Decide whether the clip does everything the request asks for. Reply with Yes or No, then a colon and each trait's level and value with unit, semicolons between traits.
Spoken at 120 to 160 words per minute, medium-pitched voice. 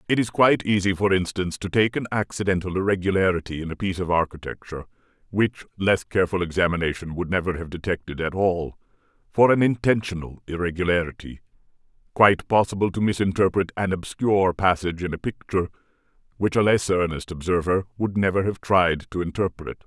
No: average, 155 wpm; very low, 95 Hz